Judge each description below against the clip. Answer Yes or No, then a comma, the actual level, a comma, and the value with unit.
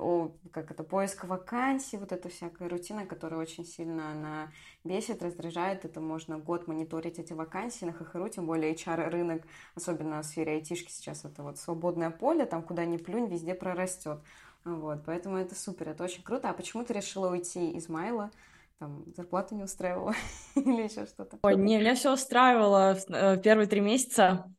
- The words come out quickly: Yes, fast, 170 wpm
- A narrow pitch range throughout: No, average, 3.2 semitones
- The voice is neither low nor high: Yes, medium, 175 Hz